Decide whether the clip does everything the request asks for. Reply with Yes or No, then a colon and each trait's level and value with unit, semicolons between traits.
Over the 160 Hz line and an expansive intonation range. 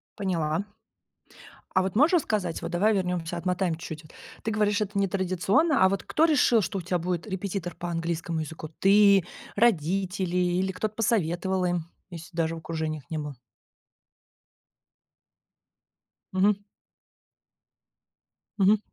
No: medium, 185 Hz; average, 3.1 semitones